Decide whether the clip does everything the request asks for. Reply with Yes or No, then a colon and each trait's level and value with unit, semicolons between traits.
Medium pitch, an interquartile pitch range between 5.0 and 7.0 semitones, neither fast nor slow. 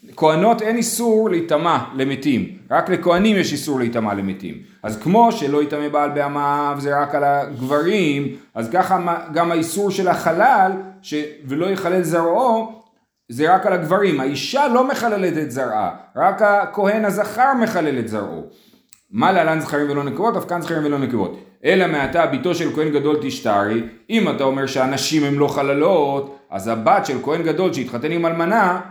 No: medium, 160 Hz; average, 5.3 semitones; fast, 165 wpm